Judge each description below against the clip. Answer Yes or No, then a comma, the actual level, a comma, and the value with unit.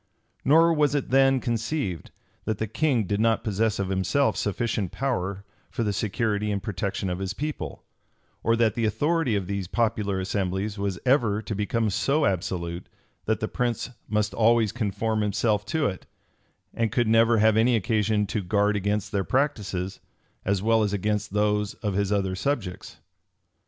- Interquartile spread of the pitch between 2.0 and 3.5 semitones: Yes, average, 2.8 semitones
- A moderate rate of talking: Yes, average, 165 wpm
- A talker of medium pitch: No, low, 105 Hz